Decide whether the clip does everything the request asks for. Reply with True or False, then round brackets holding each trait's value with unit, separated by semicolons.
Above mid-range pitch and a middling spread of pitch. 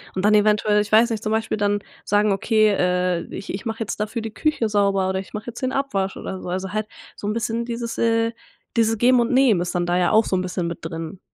True (210 Hz; 3.1 semitones)